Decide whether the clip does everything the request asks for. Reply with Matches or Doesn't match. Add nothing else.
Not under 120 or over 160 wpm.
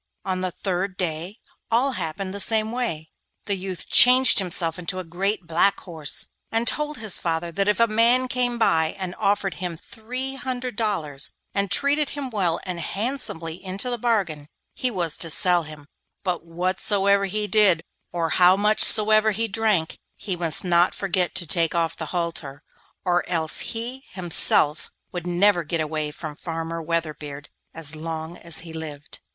Doesn't match